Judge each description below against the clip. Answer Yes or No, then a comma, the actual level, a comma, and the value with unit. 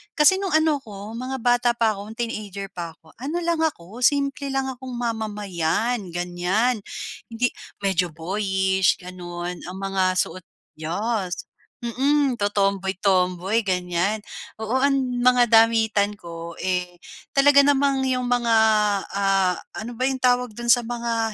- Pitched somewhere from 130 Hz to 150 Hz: No, high, 215 Hz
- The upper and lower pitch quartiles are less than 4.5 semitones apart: No, average, 5.1 semitones